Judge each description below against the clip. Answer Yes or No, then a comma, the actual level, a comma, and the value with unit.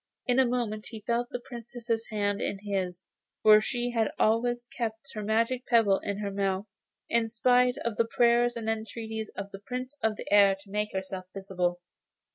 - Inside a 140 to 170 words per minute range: No, average, 185 wpm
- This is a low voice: No, high, 220 Hz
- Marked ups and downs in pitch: No, average, 2.9 semitones